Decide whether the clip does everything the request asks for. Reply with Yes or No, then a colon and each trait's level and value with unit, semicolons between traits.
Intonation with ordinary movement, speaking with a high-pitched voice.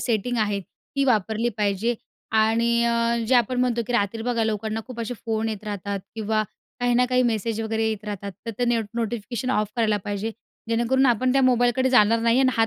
No: narrow, 2.2 semitones; high, 230 Hz